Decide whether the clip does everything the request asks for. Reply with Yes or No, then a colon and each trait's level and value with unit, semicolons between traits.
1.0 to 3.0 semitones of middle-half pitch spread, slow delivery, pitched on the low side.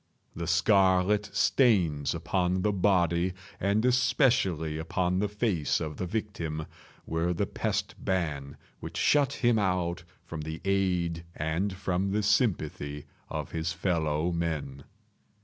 No: average, 3.8 semitones; slow, 130 wpm; very low, 90 Hz